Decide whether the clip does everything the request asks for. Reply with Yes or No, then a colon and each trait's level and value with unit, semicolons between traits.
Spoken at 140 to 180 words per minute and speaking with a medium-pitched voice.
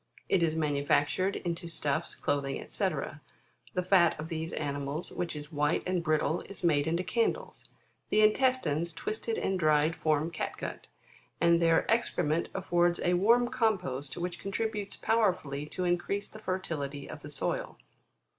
Yes: average, 155 wpm; medium, 170 Hz